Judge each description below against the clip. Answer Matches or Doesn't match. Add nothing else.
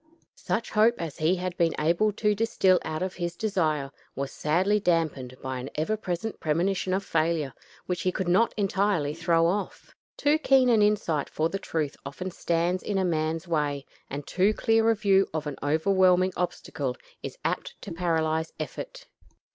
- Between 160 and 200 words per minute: Matches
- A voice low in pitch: Doesn't match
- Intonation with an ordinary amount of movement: Matches